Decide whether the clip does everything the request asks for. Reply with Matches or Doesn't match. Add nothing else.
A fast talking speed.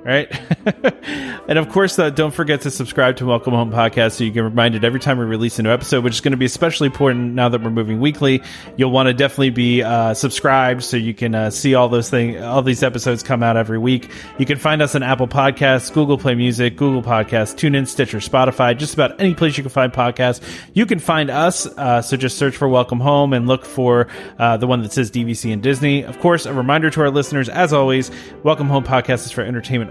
Matches